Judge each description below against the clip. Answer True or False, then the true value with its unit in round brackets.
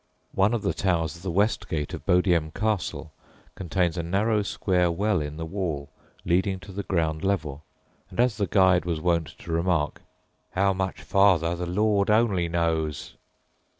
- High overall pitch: False (90 Hz)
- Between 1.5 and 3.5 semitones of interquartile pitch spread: True (3.1 semitones)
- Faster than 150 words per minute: True (170 wpm)